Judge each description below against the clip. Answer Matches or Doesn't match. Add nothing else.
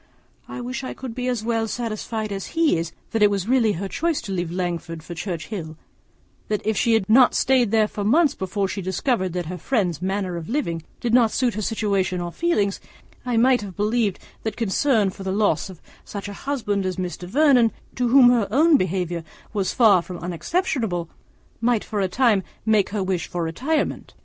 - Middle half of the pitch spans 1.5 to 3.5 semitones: Doesn't match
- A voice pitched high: Matches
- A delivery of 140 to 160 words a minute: Doesn't match